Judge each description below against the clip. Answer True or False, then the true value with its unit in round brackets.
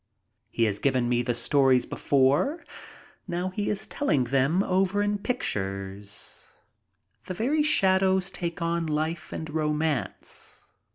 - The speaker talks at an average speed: False (125 wpm)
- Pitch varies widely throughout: True (6.7 semitones)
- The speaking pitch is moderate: True (160 Hz)